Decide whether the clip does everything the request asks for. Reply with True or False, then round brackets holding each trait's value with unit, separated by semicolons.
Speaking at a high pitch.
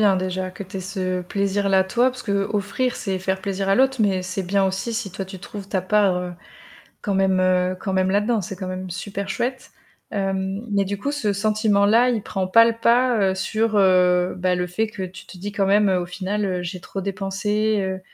True (195 Hz)